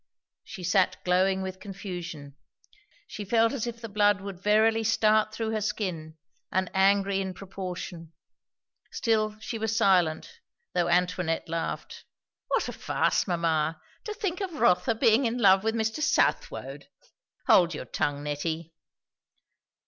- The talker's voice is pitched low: No, high, 195 Hz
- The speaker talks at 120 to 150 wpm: Yes, average, 140 wpm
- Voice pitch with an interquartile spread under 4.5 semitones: Yes, average, 4.0 semitones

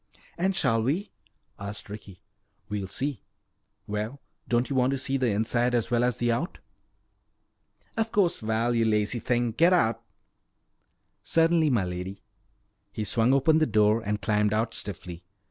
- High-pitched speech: No, low, 115 Hz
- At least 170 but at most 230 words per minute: No, average, 150 wpm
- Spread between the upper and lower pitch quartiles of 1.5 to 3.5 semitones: No, average, 4.4 semitones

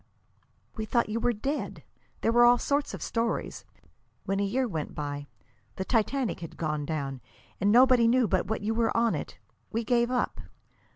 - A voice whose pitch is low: No, high, 225 Hz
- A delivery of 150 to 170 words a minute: No, average, 180 wpm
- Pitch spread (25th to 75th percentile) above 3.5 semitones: Yes, average, 4.2 semitones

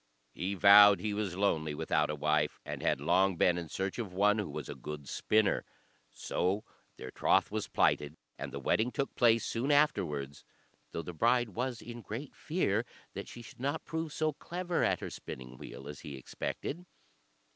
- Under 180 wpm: No, average, 185 wpm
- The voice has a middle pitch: No, low, 100 Hz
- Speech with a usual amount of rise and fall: No, wide, 7.6 semitones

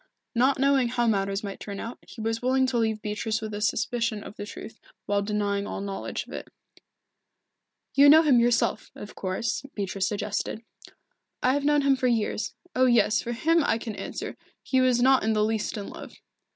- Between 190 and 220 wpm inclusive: Yes, average, 195 wpm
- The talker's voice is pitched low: No, high, 225 Hz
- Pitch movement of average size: Yes, average, 3.6 semitones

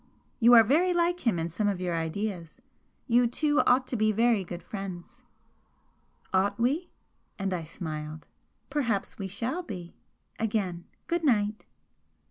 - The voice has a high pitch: Yes, high, 215 Hz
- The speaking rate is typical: Yes, average, 145 wpm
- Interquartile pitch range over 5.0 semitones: Yes, wide, 5.5 semitones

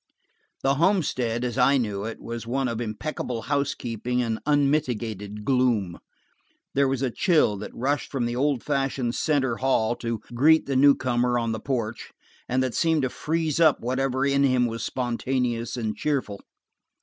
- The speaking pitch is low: Yes, low, 125 Hz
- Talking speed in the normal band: Yes, average, 165 wpm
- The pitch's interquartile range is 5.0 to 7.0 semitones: No, average, 3.1 semitones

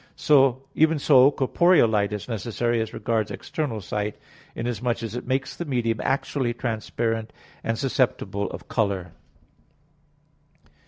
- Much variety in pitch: No, average, 3.4 semitones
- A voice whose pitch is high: No, low, 115 Hz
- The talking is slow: Yes, slow, 120 wpm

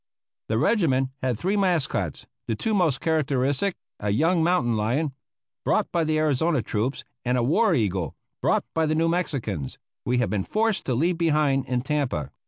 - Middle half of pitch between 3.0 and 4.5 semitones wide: No, wide, 5.4 semitones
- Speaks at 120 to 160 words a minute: No, average, 175 wpm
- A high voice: No, medium, 140 Hz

